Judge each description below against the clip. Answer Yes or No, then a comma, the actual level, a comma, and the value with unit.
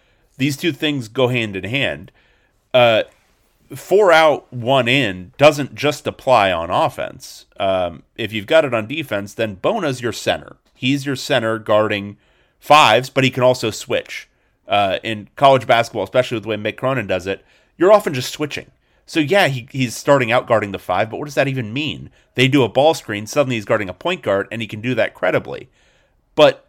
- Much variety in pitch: No, average, 4.3 semitones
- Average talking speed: Yes, average, 195 wpm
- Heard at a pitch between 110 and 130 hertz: Yes, low, 125 Hz